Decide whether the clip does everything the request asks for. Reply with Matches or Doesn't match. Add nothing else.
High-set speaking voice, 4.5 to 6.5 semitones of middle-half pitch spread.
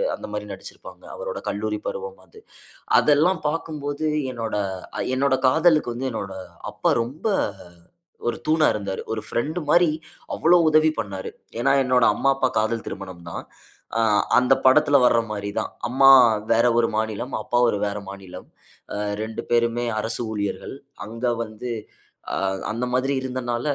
Doesn't match